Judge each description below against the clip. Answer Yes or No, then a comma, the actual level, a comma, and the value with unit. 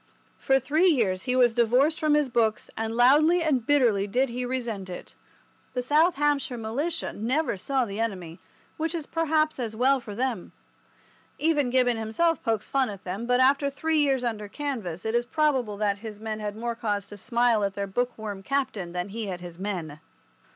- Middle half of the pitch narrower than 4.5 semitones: No, average, 5.1 semitones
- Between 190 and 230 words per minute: Yes, average, 195 wpm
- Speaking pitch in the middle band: No, high, 240 Hz